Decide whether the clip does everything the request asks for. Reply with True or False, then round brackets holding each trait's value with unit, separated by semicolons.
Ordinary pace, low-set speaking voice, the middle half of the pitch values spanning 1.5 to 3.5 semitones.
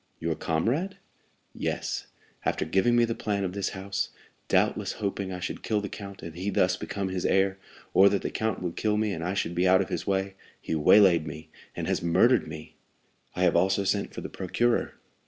False (210 wpm; 95 Hz; 2.5 semitones)